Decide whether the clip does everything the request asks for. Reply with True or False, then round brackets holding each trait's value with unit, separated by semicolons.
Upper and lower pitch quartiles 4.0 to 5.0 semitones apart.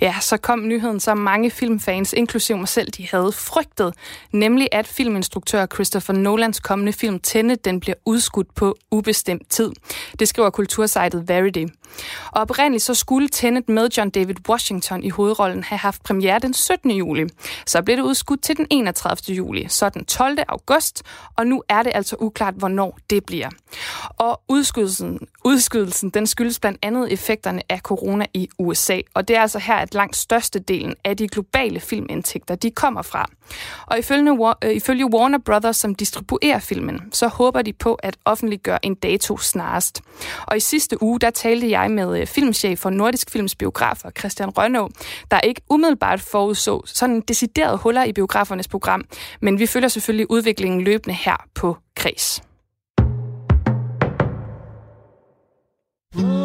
False (3.3 semitones)